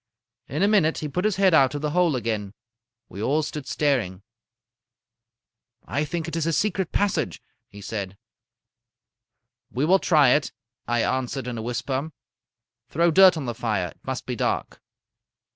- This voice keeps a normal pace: Yes, average, 165 wpm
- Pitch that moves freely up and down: Yes, wide, 5.8 semitones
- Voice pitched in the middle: Yes, medium, 145 Hz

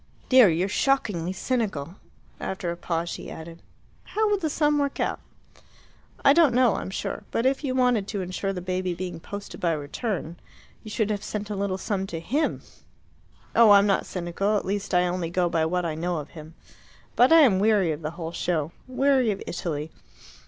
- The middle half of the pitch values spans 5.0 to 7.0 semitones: Yes, wide, 5.4 semitones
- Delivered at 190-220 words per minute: Yes, average, 195 wpm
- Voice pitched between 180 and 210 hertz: Yes, high, 190 Hz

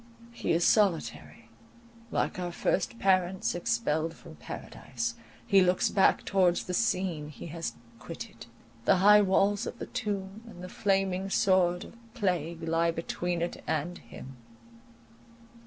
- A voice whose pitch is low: No, medium, 180 Hz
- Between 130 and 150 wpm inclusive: Yes, average, 140 wpm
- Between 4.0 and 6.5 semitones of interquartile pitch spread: No, average, 2.9 semitones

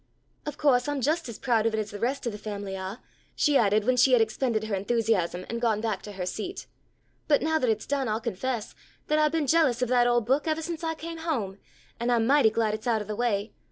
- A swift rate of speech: Yes, fast, 255 wpm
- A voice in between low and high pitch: No, high, 235 Hz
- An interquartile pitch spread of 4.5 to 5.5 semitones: Yes, average, 4.8 semitones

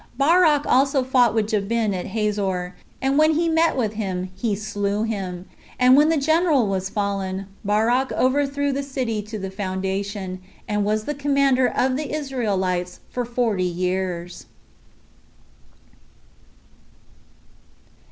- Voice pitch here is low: No, high, 220 Hz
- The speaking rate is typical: No, slow, 130 wpm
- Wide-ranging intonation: Yes, wide, 5.9 semitones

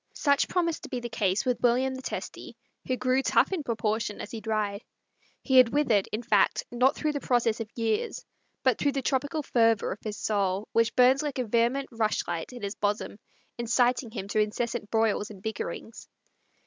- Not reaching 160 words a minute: No, average, 195 wpm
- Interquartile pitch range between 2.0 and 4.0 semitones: Yes, average, 3.3 semitones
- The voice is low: No, high, 235 Hz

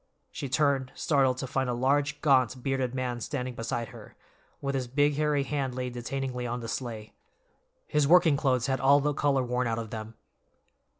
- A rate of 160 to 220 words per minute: Yes, average, 185 wpm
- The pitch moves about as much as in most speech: No, narrow, 2.3 semitones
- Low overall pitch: Yes, low, 130 Hz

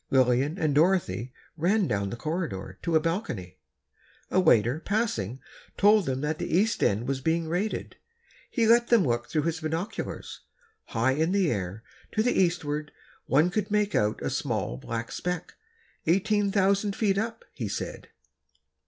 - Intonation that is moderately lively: No, wide, 7.9 semitones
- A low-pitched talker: No, medium, 160 Hz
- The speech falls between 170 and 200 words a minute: No, average, 155 wpm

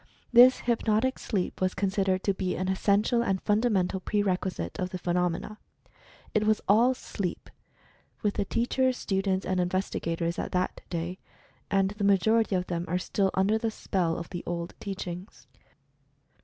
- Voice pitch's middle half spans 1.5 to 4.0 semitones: Yes, average, 2.8 semitones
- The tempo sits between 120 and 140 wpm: No, average, 165 wpm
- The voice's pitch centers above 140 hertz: Yes, high, 190 Hz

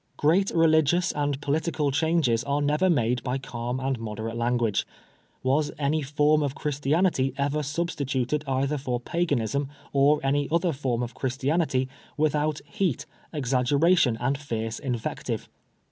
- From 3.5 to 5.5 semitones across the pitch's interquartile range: No, average, 3.1 semitones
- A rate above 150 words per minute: No, average, 140 wpm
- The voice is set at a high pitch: No, medium, 140 Hz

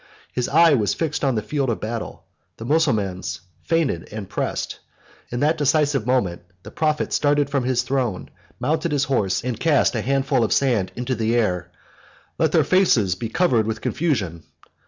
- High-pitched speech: No, low, 125 Hz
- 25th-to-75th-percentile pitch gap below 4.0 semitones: No, average, 5.2 semitones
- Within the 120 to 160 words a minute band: No, average, 180 wpm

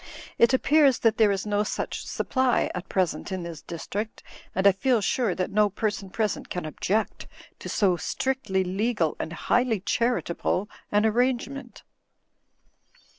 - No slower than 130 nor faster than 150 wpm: Yes, average, 145 wpm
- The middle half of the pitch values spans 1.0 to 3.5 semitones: No, average, 4.1 semitones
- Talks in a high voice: Yes, high, 210 Hz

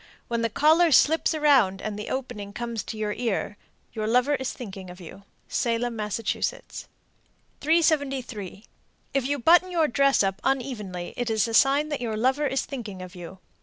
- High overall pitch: Yes, high, 240 Hz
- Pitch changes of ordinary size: Yes, average, 5.0 semitones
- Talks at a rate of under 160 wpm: No, average, 170 wpm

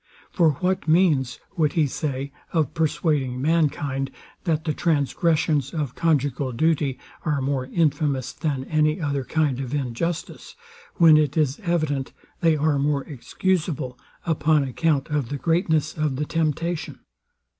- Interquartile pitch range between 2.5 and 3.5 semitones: Yes, average, 2.8 semitones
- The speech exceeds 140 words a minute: No, slow, 135 wpm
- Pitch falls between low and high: Yes, medium, 150 Hz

